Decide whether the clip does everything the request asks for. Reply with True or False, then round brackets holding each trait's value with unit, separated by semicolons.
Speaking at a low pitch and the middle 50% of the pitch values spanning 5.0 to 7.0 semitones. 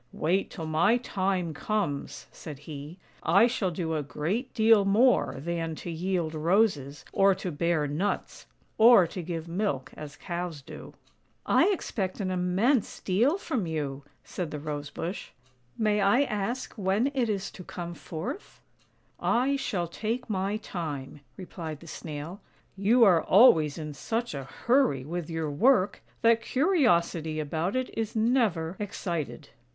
False (180 Hz; 5.6 semitones)